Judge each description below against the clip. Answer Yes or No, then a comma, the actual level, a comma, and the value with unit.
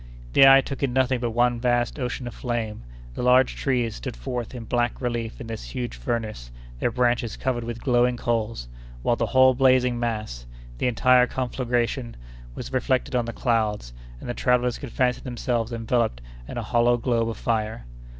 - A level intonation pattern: Yes, narrow, 1.6 semitones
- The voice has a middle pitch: No, low, 120 Hz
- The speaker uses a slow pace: No, average, 180 wpm